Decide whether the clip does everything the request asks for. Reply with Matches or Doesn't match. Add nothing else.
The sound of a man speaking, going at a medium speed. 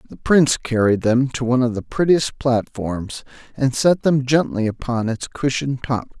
Matches